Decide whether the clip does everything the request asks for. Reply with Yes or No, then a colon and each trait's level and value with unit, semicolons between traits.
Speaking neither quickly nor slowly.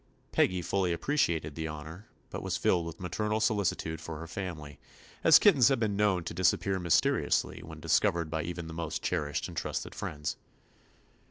Yes: average, 180 wpm